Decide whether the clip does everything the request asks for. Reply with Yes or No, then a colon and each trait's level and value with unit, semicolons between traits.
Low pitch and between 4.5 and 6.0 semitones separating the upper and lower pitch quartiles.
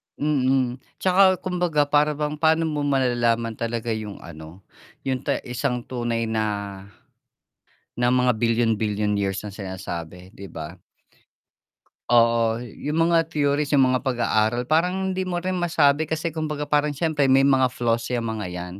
Yes: low, 125 Hz; average, 5.3 semitones